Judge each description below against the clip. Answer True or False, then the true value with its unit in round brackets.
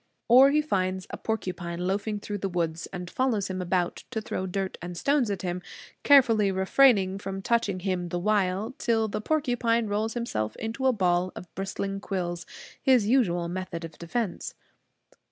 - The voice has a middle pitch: False (195 Hz)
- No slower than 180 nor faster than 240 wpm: False (170 wpm)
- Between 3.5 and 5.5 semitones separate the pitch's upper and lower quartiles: True (4.1 semitones)